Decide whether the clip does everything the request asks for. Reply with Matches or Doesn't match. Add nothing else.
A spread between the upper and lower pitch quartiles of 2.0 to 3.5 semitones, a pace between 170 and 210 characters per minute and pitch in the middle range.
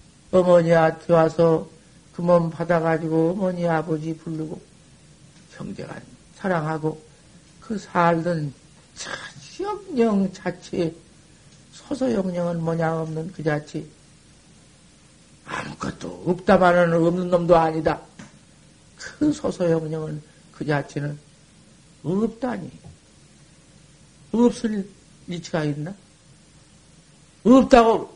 Matches